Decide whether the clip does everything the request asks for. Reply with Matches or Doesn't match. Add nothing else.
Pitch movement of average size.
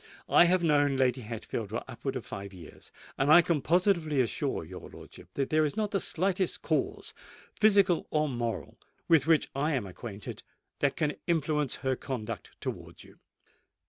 Doesn't match